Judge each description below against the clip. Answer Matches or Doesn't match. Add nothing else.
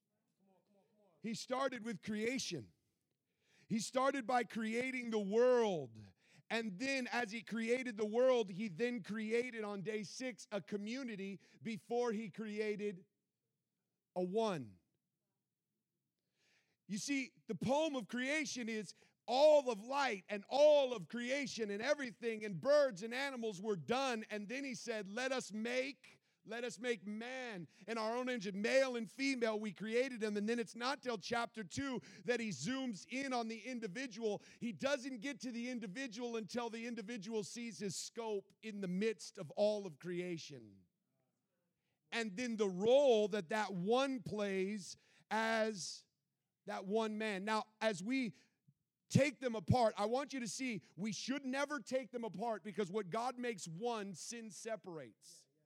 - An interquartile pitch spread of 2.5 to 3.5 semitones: Matches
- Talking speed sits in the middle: Matches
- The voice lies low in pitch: Doesn't match